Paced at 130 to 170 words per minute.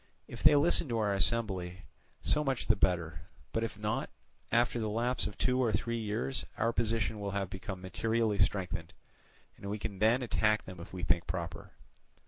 No: average, 185 wpm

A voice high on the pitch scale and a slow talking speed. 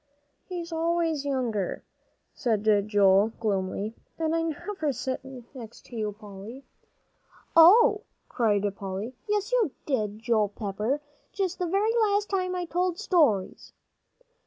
Yes: very high, 270 Hz; slow, 125 wpm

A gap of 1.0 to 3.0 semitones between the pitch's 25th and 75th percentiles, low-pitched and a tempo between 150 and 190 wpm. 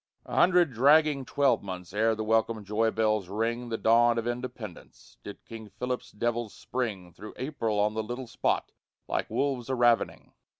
Yes: narrow, 2.6 semitones; low, 115 Hz; average, 165 wpm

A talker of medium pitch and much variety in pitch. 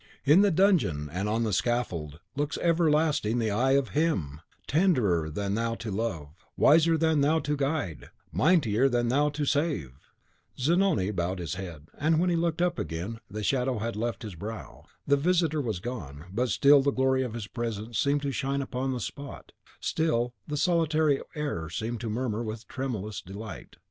No: low, 125 Hz; wide, 6.1 semitones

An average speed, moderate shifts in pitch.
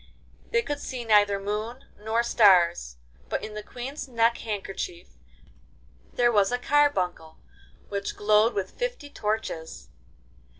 No: slow, 125 wpm; average, 3.6 semitones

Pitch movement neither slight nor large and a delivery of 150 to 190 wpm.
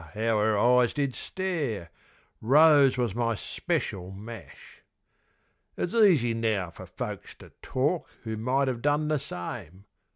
No: average, 4.9 semitones; slow, 135 wpm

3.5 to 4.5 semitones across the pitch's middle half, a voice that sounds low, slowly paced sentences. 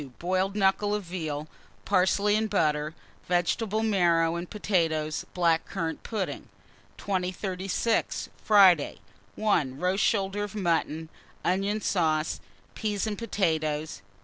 No: average, 4.0 semitones; medium, 185 Hz; slow, 115 wpm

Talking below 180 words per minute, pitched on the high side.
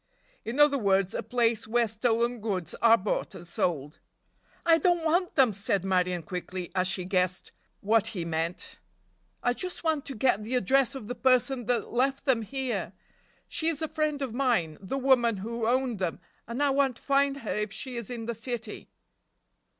No: average, 190 wpm; high, 235 Hz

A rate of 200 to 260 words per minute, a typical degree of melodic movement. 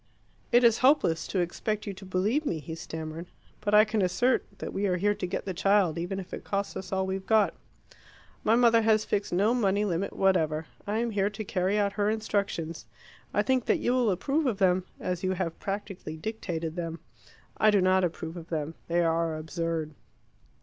Yes: fast, 205 wpm; average, 3.8 semitones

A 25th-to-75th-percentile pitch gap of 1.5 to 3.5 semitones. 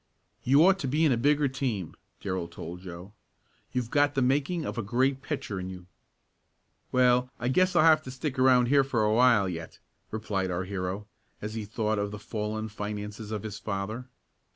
No: average, 4.6 semitones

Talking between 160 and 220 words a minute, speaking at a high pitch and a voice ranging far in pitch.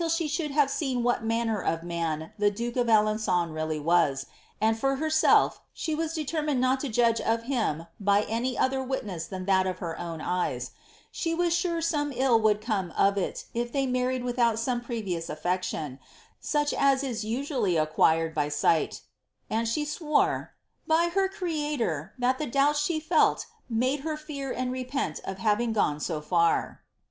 Yes: average, 180 wpm; high, 235 Hz; wide, 7.3 semitones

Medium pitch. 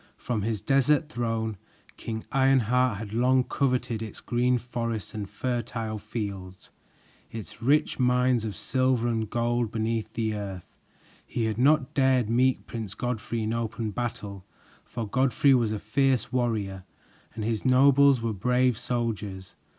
No: low, 115 Hz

